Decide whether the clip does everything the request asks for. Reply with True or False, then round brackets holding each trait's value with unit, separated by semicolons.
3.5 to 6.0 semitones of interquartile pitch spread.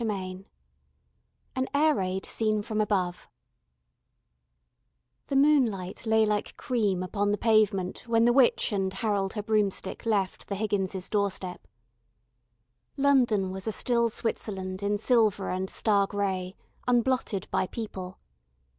False (3.0 semitones)